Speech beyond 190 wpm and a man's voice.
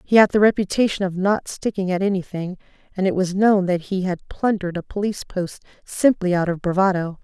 No: average, 200 wpm; female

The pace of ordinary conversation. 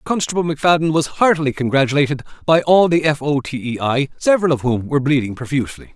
Yes: average, 190 wpm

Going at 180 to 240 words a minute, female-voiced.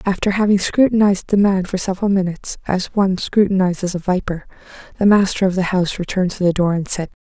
Yes: average, 200 wpm; female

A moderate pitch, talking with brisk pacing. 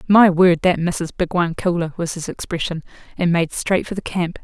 Yes: medium, 175 Hz; fast, 215 wpm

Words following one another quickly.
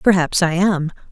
No: average, 160 wpm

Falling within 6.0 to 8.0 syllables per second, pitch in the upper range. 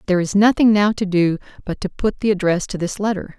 Yes: 6.1 syllables/s; high, 195 Hz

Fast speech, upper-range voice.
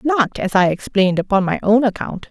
Yes: fast, 210 wpm; high, 210 Hz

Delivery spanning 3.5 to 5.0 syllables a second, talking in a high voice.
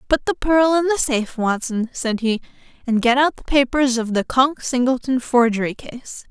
Yes: 4.9 syllables/s; very high, 255 Hz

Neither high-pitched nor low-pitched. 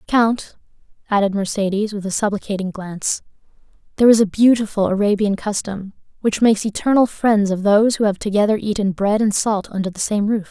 No: high, 205 Hz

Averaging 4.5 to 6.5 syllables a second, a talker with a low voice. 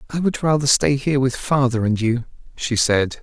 Yes: 5.2 syllables/s; low, 130 Hz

